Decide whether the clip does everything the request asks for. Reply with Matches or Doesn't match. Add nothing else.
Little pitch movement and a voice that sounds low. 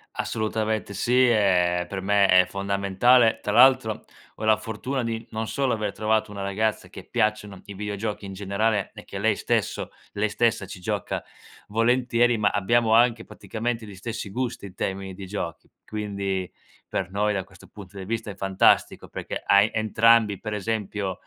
Matches